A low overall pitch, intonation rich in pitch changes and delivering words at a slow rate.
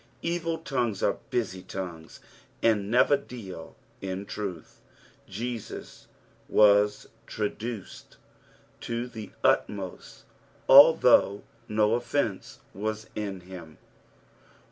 No: low, 105 Hz; average, 3.8 semitones; slow, 90 wpm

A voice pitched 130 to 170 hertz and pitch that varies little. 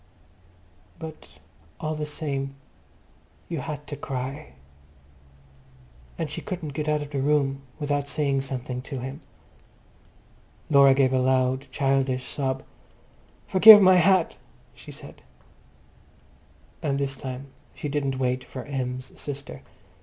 Yes: medium, 140 Hz; narrow, 2.2 semitones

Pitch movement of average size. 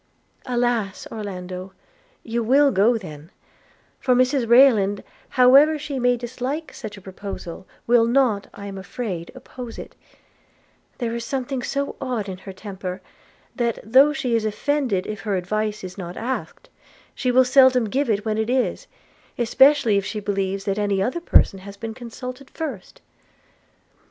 Yes: average, 4.4 semitones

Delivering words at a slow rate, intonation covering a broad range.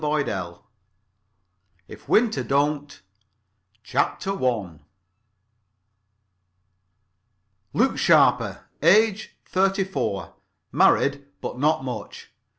Yes: slow, 75 wpm; wide, 7.1 semitones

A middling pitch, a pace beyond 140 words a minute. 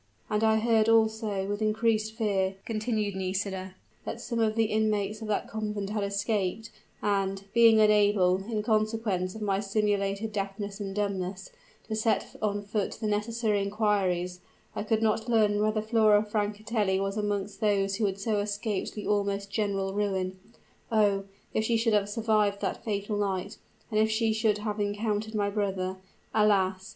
No: high, 210 Hz; average, 165 wpm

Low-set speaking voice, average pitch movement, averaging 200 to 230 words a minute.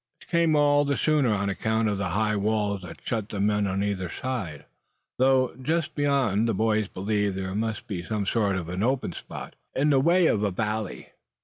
Yes: low, 110 Hz; average, 4.8 semitones; fast, 205 wpm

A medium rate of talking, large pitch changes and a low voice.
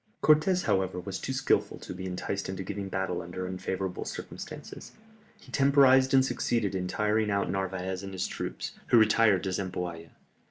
No: average, 165 wpm; average, 3.2 semitones; very low, 95 Hz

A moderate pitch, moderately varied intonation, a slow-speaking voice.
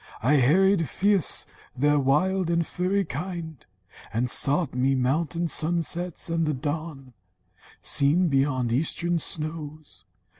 Yes: medium, 155 Hz; average, 4.0 semitones; slow, 115 wpm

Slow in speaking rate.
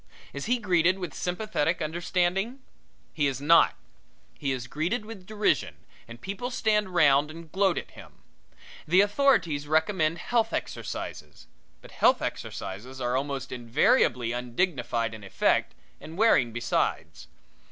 Yes: slow, 130 wpm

